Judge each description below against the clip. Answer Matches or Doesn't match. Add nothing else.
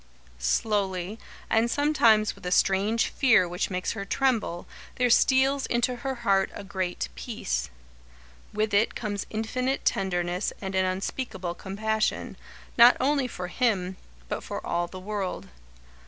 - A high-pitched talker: Matches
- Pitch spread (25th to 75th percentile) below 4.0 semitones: Doesn't match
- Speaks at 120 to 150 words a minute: Matches